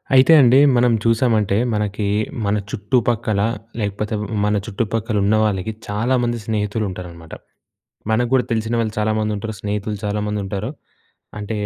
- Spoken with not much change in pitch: Yes, narrow, 2.0 semitones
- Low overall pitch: Yes, low, 110 Hz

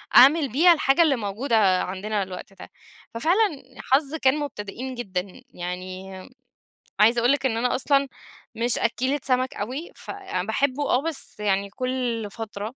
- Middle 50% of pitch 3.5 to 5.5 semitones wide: Yes, average, 5.1 semitones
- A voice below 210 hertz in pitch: No, high, 245 Hz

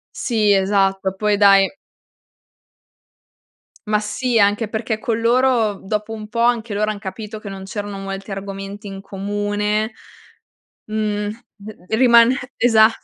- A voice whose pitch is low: No, high, 210 Hz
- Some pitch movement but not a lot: No, narrow, 1.9 semitones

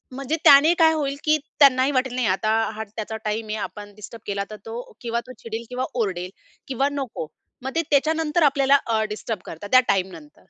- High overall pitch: Yes, very high, 250 Hz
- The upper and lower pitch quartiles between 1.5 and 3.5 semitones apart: No, average, 4.7 semitones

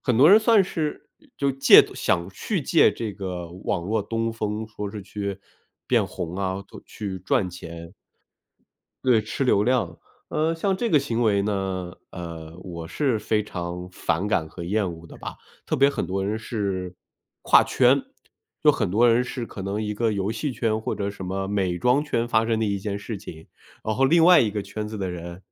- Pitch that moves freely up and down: No, average, 4.3 semitones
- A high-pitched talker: No, low, 105 Hz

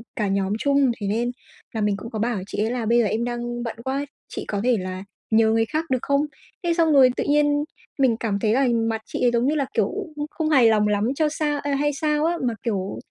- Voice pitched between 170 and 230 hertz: No, high, 240 Hz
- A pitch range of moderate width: Yes, average, 4.7 semitones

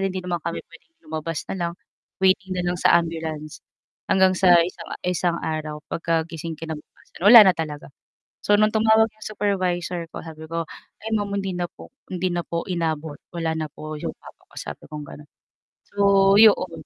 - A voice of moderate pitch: Yes, medium, 175 Hz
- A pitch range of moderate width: Yes, average, 3.3 semitones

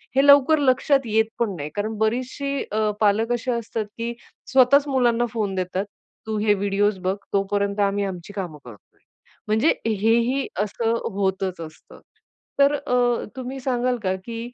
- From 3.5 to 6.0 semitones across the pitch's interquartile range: Yes, average, 3.8 semitones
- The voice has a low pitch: No, high, 220 Hz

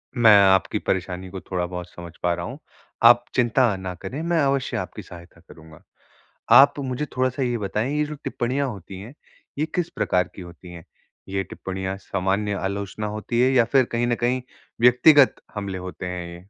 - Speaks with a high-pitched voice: No, low, 105 Hz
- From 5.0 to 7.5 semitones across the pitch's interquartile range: Yes, wide, 5.5 semitones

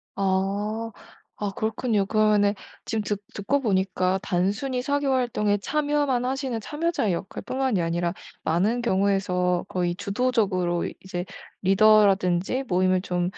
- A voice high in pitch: Yes, high, 205 Hz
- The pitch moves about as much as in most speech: Yes, average, 4.6 semitones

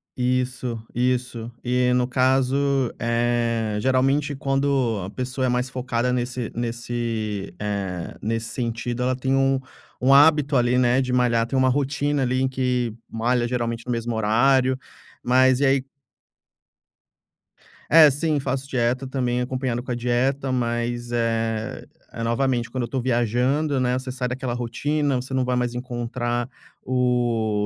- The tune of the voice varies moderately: No, narrow, 1.7 semitones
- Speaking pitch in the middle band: No, low, 125 Hz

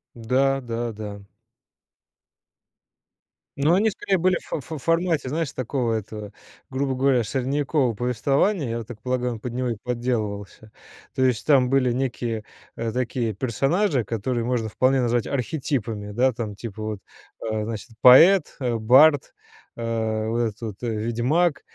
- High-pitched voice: No, low, 125 Hz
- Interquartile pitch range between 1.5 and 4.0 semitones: Yes, average, 3.4 semitones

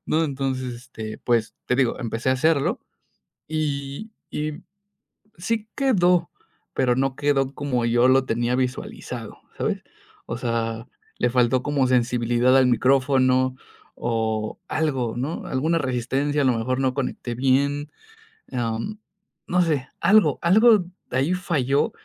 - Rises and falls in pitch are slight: No, average, 3.2 semitones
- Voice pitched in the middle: No, low, 130 Hz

